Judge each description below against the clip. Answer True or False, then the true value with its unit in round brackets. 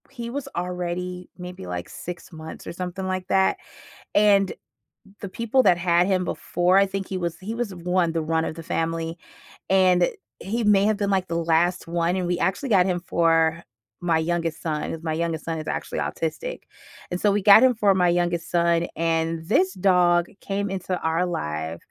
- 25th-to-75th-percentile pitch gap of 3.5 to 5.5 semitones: False (2.5 semitones)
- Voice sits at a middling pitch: True (180 Hz)